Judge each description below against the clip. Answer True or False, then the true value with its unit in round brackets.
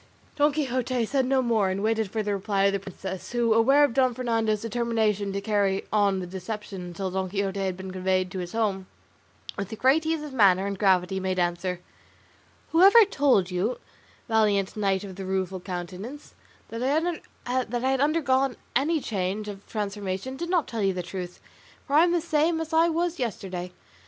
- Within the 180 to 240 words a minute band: True (185 wpm)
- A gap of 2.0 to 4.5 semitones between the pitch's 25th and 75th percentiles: False (5.5 semitones)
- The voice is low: False (210 Hz)